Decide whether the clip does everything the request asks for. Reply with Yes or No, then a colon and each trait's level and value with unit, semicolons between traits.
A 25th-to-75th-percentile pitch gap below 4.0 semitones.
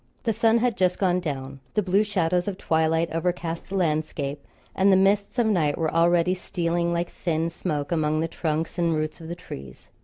Yes: average, 2.8 semitones